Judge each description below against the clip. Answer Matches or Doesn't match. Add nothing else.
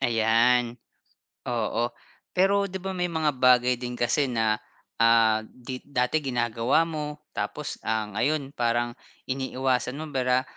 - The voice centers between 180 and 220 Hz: Doesn't match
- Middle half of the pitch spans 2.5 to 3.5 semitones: Doesn't match